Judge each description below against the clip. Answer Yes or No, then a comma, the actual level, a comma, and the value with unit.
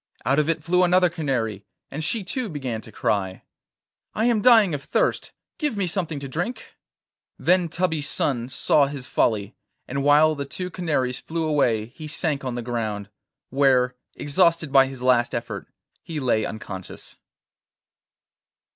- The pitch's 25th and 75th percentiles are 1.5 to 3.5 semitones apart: No, average, 5.2 semitones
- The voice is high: No, medium, 145 Hz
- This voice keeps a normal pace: Yes, average, 155 wpm